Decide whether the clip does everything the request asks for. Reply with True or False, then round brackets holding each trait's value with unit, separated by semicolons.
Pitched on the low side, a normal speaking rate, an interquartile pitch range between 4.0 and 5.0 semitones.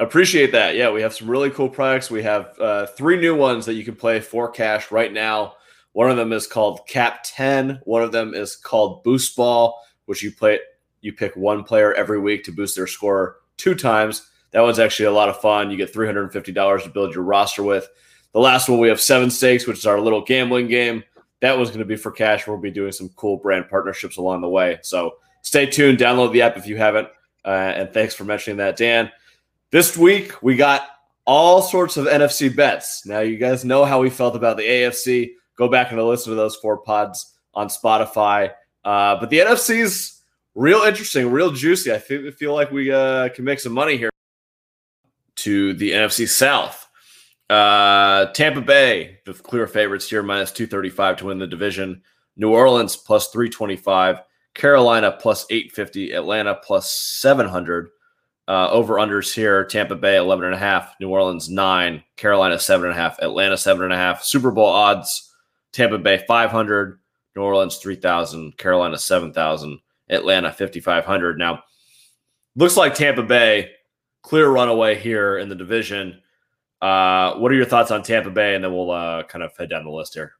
True (110 Hz; 185 wpm; 4.3 semitones)